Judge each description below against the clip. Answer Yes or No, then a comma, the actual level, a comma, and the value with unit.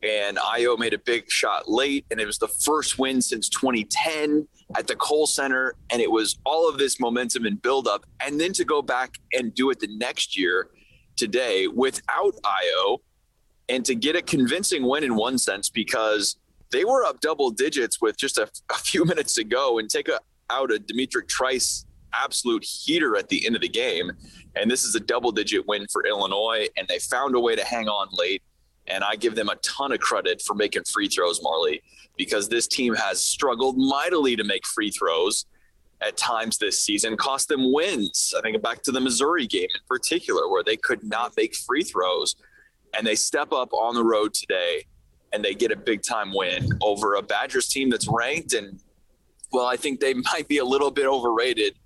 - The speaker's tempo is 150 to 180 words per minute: No, average, 200 wpm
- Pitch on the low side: No, very high, 360 Hz